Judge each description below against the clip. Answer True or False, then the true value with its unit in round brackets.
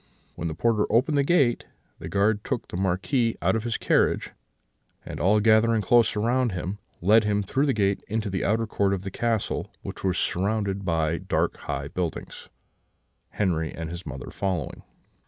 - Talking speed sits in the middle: True (175 wpm)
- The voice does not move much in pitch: False (3.7 semitones)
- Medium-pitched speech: False (105 Hz)